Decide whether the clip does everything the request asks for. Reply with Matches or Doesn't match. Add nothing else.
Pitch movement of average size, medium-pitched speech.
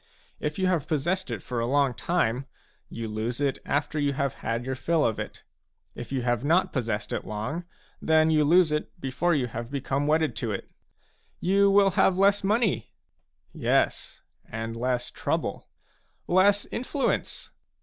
Doesn't match